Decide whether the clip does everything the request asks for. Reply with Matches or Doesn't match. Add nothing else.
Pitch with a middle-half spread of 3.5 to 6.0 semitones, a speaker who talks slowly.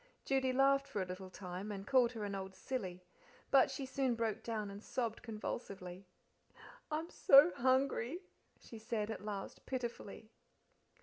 Doesn't match